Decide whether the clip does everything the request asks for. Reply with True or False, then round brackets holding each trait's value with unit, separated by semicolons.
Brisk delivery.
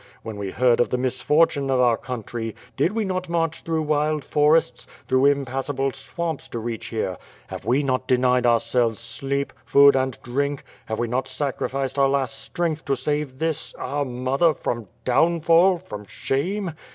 False (165 wpm)